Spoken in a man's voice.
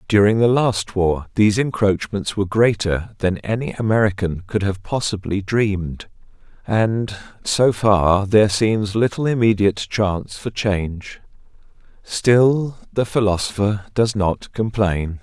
Yes: male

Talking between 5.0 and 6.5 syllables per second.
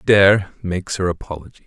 Yes: 6.0 syllables/s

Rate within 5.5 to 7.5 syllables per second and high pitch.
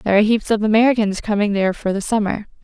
Yes: 6.9 syllables/s; high, 210 Hz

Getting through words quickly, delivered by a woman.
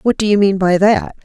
Yes: fast, 290 wpm; female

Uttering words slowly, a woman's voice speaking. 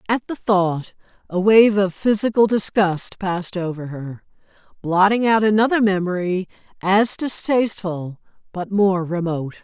Yes: slow, 125 wpm; female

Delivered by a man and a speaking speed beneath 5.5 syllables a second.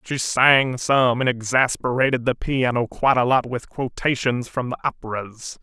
Yes: male; 4.6 syllables/s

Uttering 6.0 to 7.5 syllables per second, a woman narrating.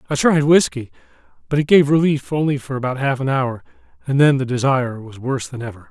No: 6.2 syllables/s; male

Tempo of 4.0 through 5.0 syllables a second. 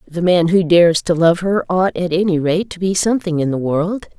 No: 5.4 syllables/s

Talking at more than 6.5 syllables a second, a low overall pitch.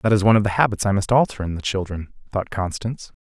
Yes: 6.8 syllables/s; low, 105 Hz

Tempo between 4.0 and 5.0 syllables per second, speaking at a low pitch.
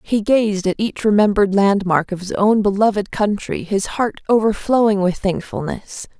No: 4.7 syllables/s; high, 205 Hz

